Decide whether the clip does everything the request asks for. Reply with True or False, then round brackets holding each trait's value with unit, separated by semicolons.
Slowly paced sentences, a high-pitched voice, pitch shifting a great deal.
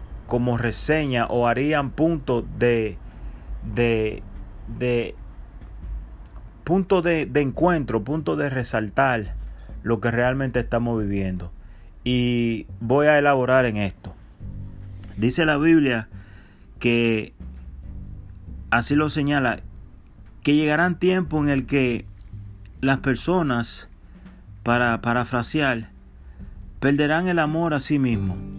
False (105 wpm; 120 Hz; 6.4 semitones)